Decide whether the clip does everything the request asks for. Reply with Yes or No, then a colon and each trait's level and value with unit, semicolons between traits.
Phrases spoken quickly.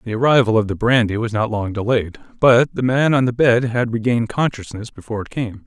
Yes: fast, 210 wpm